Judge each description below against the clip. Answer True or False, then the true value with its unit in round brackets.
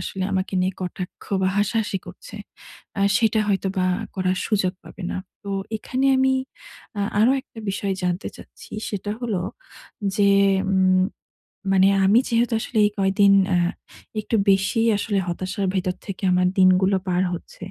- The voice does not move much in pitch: True (2.2 semitones)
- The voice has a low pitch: False (195 Hz)